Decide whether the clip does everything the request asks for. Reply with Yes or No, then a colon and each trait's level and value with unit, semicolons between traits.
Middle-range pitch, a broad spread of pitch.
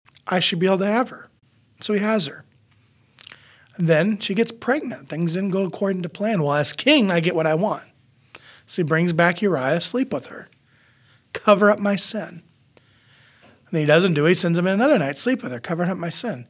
Yes: medium, 175 Hz; wide, 6.4 semitones